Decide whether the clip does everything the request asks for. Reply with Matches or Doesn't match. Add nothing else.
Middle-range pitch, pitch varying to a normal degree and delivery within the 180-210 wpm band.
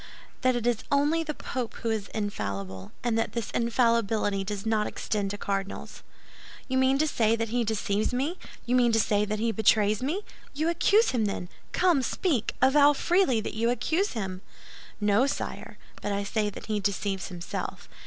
Doesn't match